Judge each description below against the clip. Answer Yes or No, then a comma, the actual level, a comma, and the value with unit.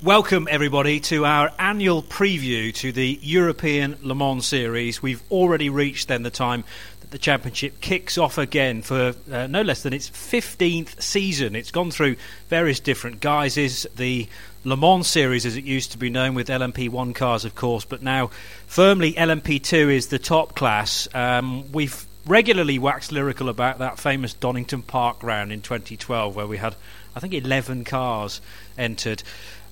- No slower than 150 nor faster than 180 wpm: Yes, average, 165 wpm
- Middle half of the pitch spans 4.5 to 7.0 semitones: No, average, 3.8 semitones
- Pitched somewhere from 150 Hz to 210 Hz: No, low, 130 Hz